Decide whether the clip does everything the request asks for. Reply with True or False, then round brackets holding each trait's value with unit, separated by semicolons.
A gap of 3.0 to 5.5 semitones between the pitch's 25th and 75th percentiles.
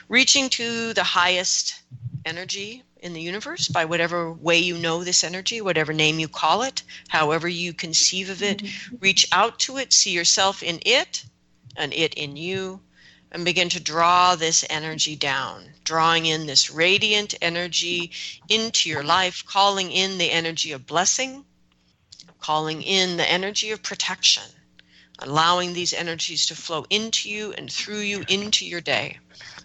True (3.4 semitones)